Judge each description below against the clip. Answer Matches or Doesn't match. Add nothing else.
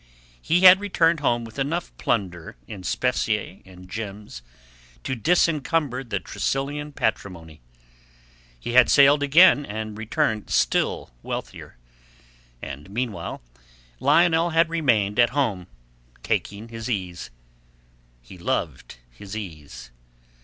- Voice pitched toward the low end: Matches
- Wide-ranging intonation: Matches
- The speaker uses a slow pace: Matches